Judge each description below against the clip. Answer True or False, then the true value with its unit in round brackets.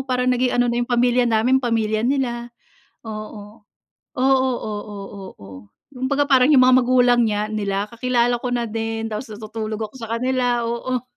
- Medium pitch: False (240 Hz)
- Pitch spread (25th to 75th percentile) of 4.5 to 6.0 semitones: False (2.5 semitones)